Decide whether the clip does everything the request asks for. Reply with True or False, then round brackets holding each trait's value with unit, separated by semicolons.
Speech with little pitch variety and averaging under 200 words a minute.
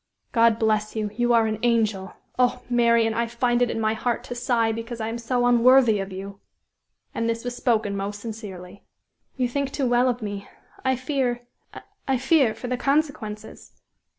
True (2.2 semitones; 180 wpm)